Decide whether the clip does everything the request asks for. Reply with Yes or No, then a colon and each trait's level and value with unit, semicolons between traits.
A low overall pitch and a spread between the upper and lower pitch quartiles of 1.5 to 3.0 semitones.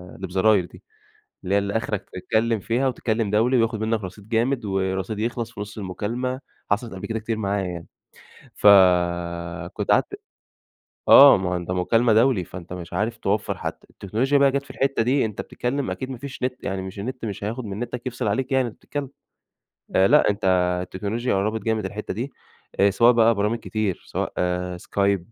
No: low, 110 Hz; average, 3.6 semitones